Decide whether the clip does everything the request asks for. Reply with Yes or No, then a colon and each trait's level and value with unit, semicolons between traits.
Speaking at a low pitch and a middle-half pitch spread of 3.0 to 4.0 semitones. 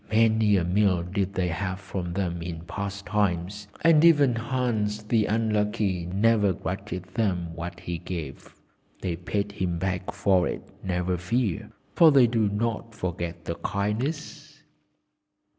Yes: low, 100 Hz; average, 3.6 semitones